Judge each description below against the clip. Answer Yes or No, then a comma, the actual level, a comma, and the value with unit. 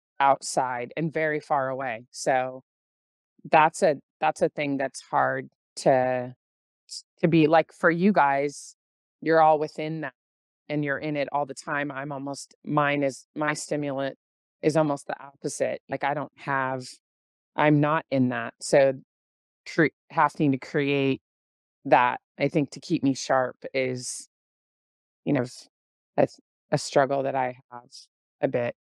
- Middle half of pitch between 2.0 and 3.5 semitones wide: Yes, average, 3.1 semitones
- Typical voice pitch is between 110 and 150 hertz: Yes, low, 135 Hz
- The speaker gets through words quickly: No, average, 150 wpm